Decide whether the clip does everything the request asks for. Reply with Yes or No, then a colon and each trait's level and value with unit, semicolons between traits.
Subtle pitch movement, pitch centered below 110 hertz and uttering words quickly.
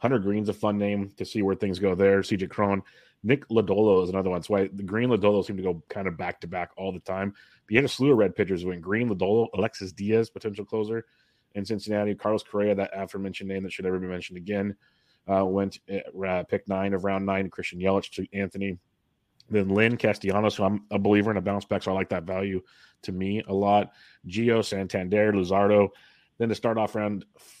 Yes: narrow, 1.7 semitones; low, 100 Hz; fast, 225 wpm